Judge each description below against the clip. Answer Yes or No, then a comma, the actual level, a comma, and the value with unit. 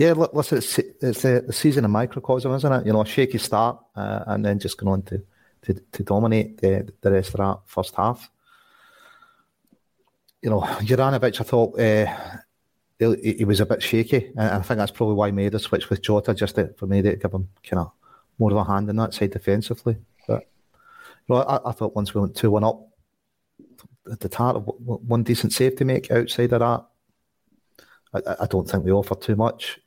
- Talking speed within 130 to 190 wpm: No, fast, 205 wpm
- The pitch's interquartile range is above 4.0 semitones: No, average, 3.3 semitones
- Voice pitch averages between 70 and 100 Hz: No, low, 110 Hz